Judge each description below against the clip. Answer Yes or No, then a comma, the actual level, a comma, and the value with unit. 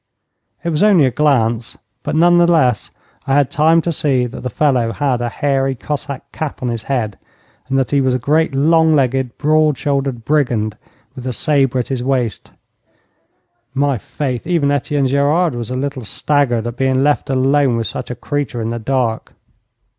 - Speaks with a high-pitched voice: No, low, 135 Hz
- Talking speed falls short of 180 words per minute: No, average, 185 wpm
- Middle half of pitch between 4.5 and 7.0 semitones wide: No, average, 3.1 semitones